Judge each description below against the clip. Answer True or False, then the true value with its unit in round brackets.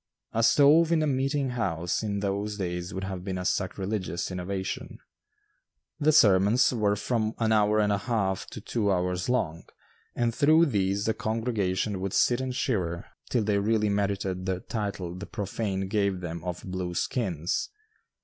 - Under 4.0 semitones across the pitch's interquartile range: True (3.5 semitones)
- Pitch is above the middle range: False (100 Hz)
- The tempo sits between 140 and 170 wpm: True (165 wpm)